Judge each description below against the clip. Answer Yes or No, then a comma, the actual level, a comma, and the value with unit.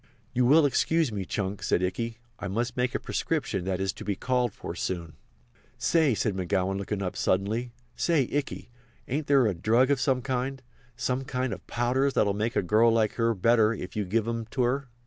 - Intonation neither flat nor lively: Yes, average, 4.3 semitones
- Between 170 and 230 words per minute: Yes, average, 200 wpm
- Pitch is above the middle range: No, low, 115 Hz